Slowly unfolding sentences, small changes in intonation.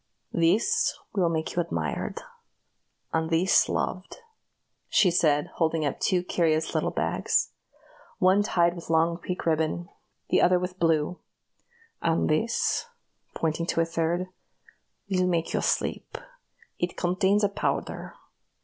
Yes: slow, 130 wpm; narrow, 2.0 semitones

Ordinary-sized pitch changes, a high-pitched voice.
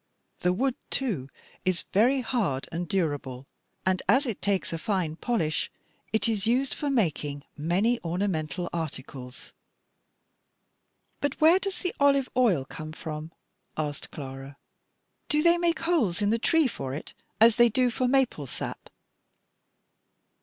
No: wide, 8.7 semitones; high, 195 Hz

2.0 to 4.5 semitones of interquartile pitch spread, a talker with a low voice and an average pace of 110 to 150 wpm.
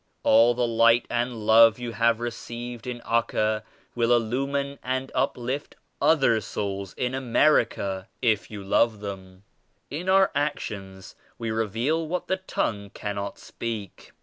Yes: average, 3.2 semitones; low, 115 Hz; average, 140 wpm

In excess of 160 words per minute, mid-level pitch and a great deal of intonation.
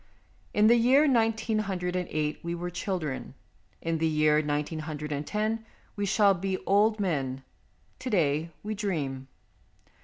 No: average, 155 wpm; medium, 180 Hz; wide, 5.8 semitones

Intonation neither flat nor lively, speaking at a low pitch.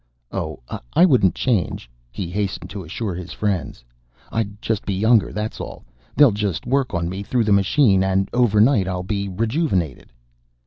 Yes: average, 3.2 semitones; low, 100 Hz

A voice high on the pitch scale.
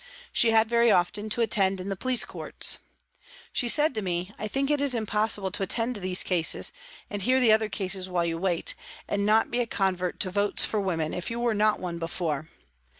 Yes: high, 205 Hz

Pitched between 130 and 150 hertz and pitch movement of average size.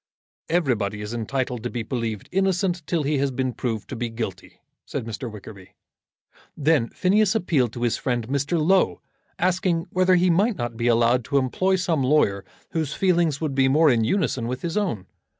No: low, 135 Hz; wide, 6.8 semitones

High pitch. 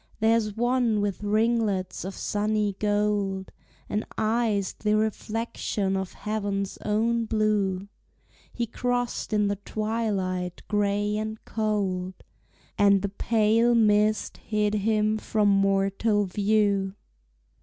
Yes: high, 210 Hz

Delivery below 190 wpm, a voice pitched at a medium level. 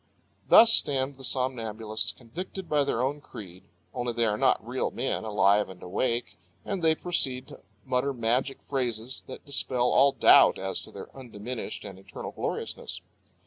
No: average, 160 wpm; low, 125 Hz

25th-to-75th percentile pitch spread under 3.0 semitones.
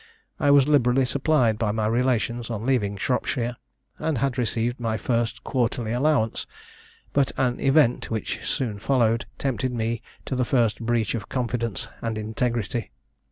Yes: narrow, 2.5 semitones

